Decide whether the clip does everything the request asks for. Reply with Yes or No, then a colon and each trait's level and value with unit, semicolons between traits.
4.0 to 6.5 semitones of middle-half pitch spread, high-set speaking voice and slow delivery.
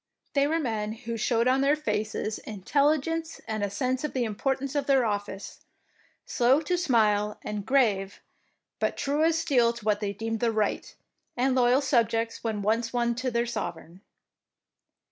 No: average, 4.3 semitones; high, 235 Hz; average, 165 wpm